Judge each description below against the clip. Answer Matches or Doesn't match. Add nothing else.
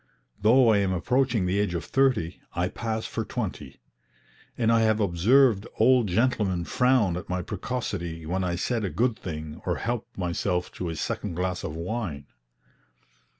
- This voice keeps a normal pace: Matches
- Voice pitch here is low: Matches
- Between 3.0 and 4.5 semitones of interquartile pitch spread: Doesn't match